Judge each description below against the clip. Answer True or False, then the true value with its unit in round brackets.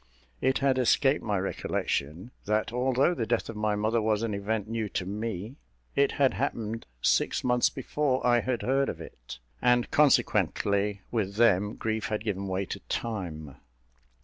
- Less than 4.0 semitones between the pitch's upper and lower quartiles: True (3.5 semitones)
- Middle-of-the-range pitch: False (110 Hz)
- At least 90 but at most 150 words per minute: False (165 wpm)